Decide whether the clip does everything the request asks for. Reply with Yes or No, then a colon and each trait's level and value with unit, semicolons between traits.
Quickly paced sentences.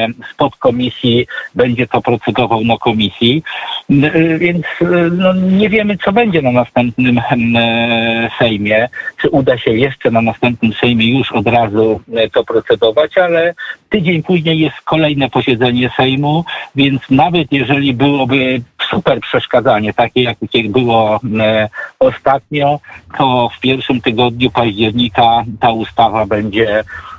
No: average, 115 wpm